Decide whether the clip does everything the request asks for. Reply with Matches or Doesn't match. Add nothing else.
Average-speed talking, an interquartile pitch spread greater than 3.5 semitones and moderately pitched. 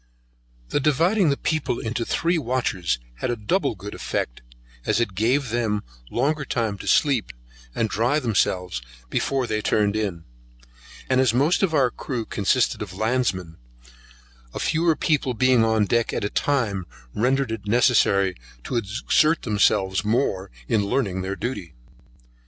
Doesn't match